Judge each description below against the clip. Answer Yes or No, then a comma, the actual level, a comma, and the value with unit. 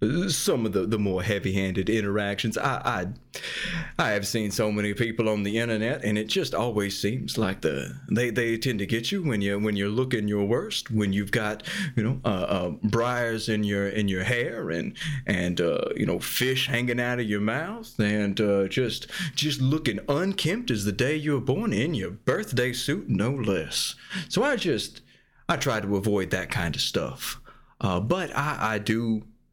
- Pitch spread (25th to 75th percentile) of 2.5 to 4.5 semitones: Yes, average, 3.7 semitones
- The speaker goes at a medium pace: Yes, average, 195 wpm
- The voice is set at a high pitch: No, low, 115 Hz